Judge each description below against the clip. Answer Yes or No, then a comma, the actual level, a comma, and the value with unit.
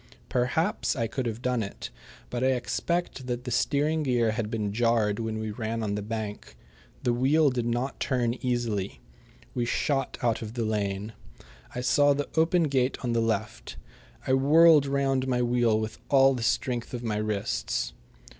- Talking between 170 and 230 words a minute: Yes, average, 175 wpm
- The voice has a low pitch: Yes, low, 120 Hz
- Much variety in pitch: No, average, 3.3 semitones